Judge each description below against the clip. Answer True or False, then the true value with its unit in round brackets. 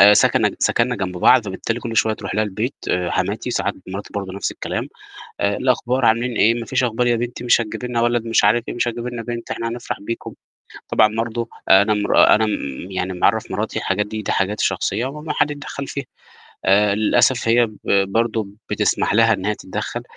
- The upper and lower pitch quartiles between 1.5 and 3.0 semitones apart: True (2.7 semitones)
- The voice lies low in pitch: True (115 Hz)